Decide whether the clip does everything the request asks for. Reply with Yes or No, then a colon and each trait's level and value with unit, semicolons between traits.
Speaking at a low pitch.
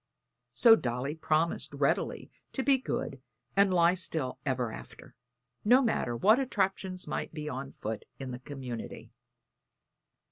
No: medium, 160 Hz